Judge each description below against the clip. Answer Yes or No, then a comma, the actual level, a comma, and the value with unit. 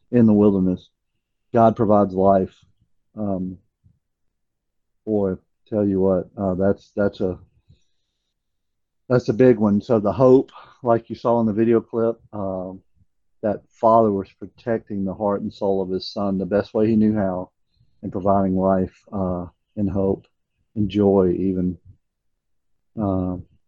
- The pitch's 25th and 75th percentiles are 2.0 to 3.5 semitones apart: Yes, narrow, 2.6 semitones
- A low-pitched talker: Yes, low, 100 Hz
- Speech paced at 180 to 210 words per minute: No, average, 145 wpm